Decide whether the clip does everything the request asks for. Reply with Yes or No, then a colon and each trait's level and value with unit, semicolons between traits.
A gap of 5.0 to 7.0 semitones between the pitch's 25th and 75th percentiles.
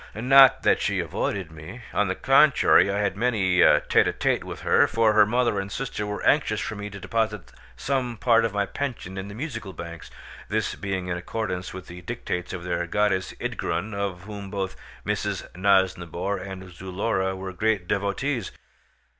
No: average, 3.1 semitones